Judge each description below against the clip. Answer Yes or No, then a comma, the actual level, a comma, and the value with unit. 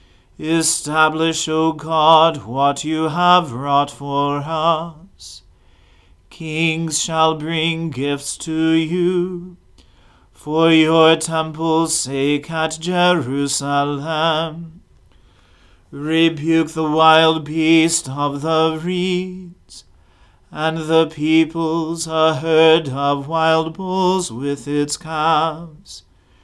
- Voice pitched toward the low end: No, medium, 160 Hz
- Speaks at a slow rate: Yes, slow, 90 wpm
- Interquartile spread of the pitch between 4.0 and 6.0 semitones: No, narrow, 2.4 semitones